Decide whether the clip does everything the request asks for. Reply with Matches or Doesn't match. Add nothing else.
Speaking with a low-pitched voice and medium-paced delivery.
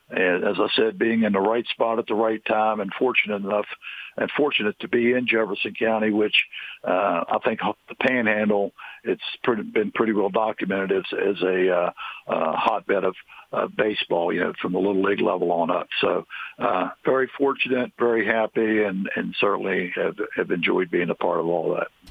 Matches